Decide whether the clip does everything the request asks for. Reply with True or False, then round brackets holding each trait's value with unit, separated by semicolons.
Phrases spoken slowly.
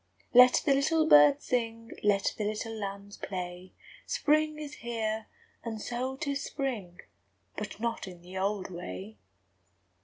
False (145 wpm)